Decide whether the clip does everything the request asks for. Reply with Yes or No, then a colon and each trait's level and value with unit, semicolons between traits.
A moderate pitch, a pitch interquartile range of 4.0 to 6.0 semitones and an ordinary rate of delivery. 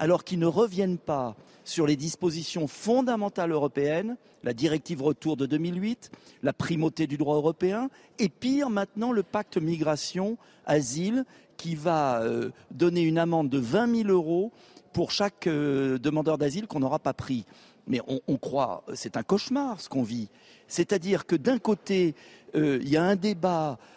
Yes: medium, 165 Hz; average, 5.2 semitones; average, 165 wpm